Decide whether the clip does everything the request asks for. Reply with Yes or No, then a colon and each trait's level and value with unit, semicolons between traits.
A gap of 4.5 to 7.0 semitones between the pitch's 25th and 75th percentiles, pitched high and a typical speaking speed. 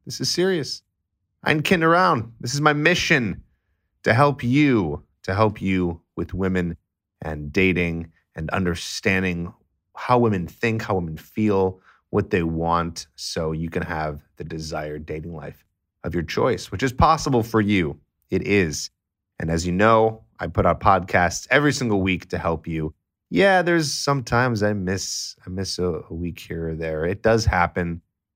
No: average, 5.2 semitones; very low, 95 Hz; average, 165 wpm